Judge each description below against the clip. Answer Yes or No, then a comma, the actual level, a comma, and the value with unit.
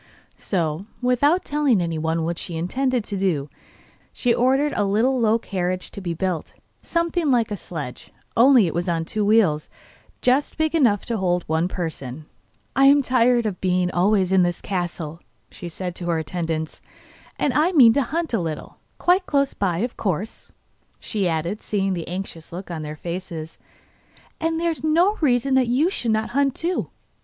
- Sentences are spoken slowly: No, average, 180 wpm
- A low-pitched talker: No, high, 200 Hz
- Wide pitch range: Yes, wide, 7.3 semitones